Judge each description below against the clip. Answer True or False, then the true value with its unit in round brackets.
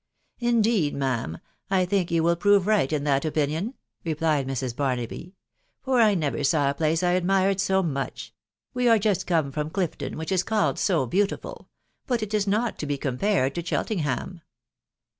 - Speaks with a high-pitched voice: False (170 Hz)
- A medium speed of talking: True (185 wpm)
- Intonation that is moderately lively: False (5.9 semitones)